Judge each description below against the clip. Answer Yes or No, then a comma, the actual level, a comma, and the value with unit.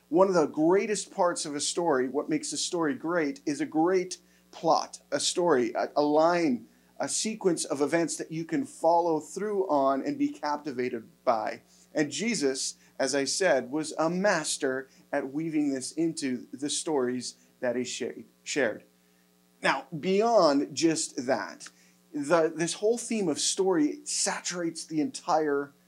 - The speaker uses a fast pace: No, average, 155 wpm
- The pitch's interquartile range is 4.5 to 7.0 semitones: Yes, average, 5.3 semitones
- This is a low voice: No, medium, 155 Hz